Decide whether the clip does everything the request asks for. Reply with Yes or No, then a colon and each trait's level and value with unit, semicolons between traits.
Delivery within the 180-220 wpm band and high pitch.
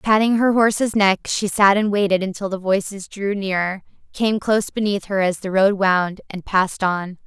Yes: average, 200 wpm; high, 200 Hz